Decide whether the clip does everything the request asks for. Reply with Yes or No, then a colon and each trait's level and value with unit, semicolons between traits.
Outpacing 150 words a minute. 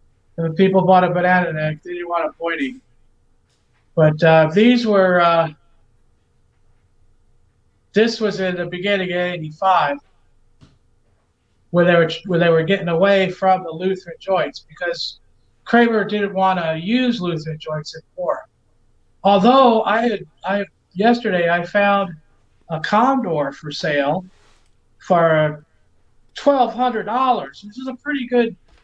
No: slow, 135 wpm